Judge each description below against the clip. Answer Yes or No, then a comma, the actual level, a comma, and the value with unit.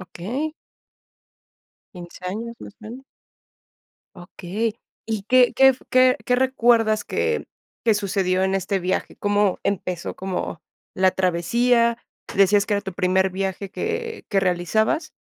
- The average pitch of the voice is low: No, high, 200 Hz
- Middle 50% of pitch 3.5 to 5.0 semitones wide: Yes, average, 4.0 semitones